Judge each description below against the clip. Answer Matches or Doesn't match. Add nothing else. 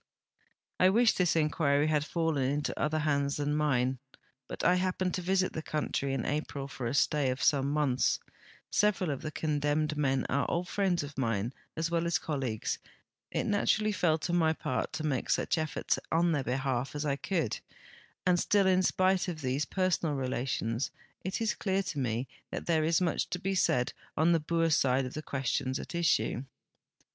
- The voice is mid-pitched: Matches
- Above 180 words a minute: Matches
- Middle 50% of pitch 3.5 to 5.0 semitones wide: Matches